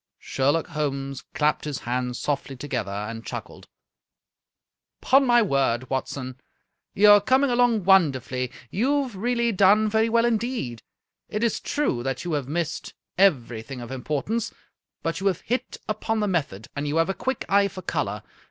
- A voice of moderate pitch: Yes, medium, 165 Hz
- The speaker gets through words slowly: No, average, 170 wpm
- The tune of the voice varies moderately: No, wide, 8.7 semitones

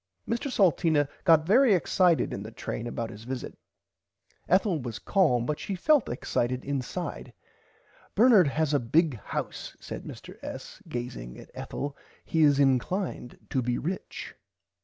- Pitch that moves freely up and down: Yes, wide, 7.0 semitones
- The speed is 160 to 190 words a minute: No, average, 145 wpm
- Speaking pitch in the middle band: Yes, medium, 145 Hz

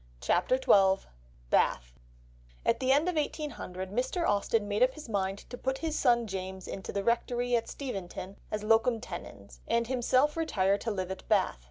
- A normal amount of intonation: Yes, average, 4.9 semitones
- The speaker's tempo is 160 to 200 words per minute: Yes, average, 175 wpm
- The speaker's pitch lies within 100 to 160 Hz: No, high, 230 Hz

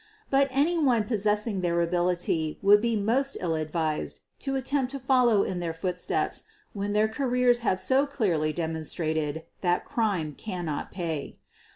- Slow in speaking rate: No, average, 145 wpm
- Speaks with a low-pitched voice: No, high, 200 Hz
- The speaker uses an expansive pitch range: Yes, wide, 6.9 semitones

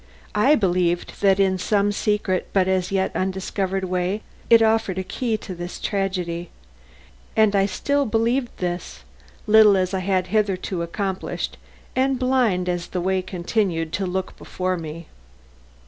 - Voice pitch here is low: No, high, 190 Hz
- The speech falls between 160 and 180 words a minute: No, average, 145 wpm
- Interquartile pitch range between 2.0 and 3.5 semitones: Yes, average, 2.7 semitones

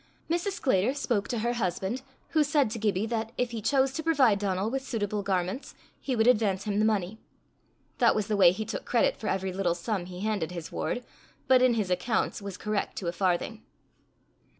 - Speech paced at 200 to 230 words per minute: Yes, fast, 205 wpm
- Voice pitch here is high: Yes, high, 215 Hz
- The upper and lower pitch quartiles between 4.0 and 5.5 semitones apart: Yes, average, 4.5 semitones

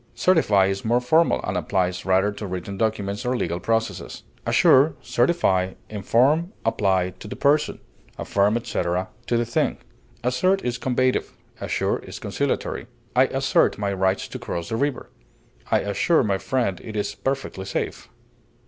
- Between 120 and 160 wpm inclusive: Yes, average, 150 wpm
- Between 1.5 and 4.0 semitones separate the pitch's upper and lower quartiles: No, average, 4.9 semitones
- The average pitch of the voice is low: Yes, low, 110 Hz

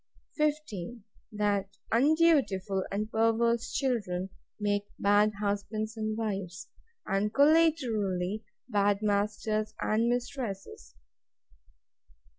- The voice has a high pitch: Yes, high, 215 Hz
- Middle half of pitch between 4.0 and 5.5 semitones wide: No, average, 2.7 semitones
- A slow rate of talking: Yes, slow, 80 wpm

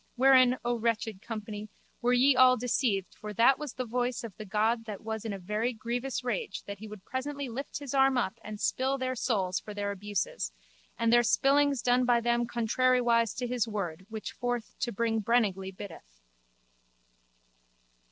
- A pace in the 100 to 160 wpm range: No, average, 180 wpm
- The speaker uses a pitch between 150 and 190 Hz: No, high, 235 Hz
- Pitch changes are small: No, average, 3.1 semitones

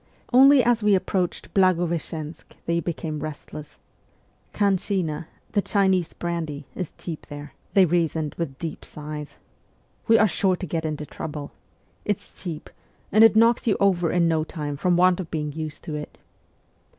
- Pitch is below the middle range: No, medium, 170 Hz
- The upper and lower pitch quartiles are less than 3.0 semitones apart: No, average, 3.8 semitones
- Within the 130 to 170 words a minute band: Yes, average, 165 wpm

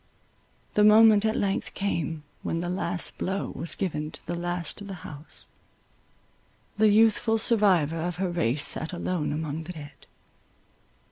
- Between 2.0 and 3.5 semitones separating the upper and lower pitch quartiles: No, average, 4.1 semitones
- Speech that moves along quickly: No, average, 150 wpm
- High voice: No, medium, 175 Hz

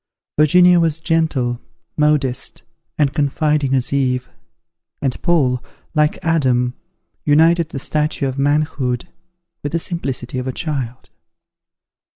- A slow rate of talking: Yes, slow, 115 wpm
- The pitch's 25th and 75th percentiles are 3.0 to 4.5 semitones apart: Yes, average, 3.5 semitones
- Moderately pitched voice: Yes, medium, 145 Hz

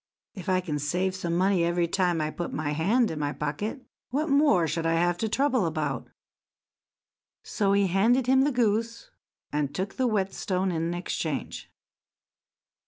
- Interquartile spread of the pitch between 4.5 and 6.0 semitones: Yes, average, 5.2 semitones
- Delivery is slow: No, average, 165 wpm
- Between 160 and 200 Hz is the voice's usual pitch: Yes, medium, 185 Hz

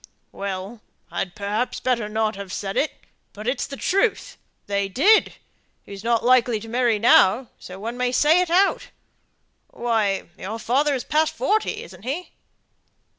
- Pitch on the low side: No, high, 235 Hz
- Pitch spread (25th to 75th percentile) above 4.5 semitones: Yes, average, 5.2 semitones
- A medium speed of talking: Yes, average, 155 wpm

